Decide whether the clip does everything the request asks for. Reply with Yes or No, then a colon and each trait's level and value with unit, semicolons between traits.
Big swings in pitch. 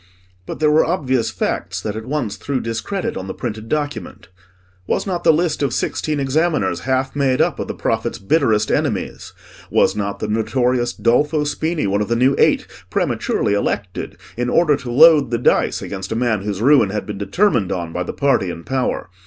Yes: wide, 6.0 semitones